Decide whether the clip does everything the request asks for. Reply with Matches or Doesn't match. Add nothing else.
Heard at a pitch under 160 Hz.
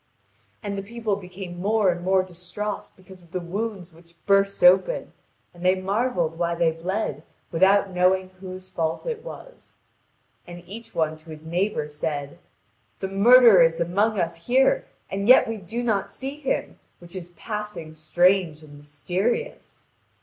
Doesn't match